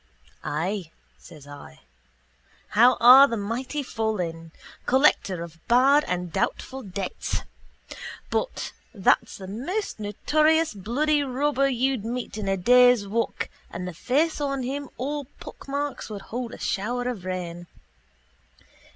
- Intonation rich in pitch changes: Yes, wide, 6.3 semitones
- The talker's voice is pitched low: No, high, 235 Hz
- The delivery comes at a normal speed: No, slow, 125 wpm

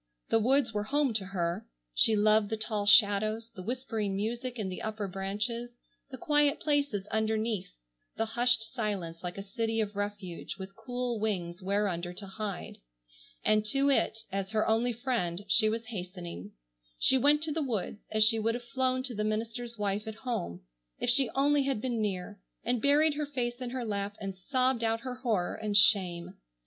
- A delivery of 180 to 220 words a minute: Yes, average, 185 wpm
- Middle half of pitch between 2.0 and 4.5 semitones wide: Yes, average, 3.6 semitones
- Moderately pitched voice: No, high, 220 Hz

